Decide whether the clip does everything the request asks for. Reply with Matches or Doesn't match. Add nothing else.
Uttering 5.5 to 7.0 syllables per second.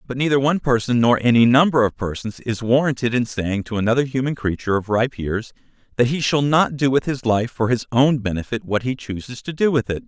Matches